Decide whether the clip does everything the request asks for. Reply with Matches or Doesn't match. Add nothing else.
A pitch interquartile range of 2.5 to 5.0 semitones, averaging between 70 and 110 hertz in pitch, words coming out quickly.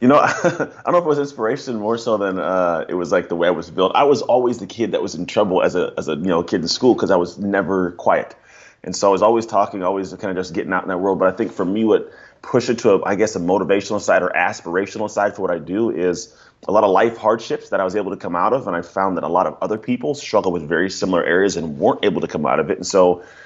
Matches